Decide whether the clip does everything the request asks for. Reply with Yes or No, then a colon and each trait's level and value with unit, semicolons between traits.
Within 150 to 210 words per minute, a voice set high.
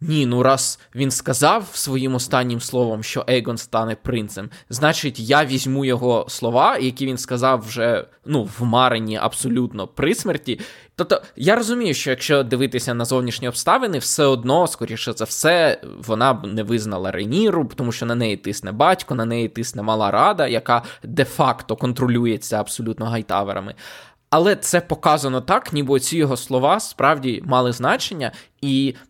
No: fast, 155 wpm; low, 125 Hz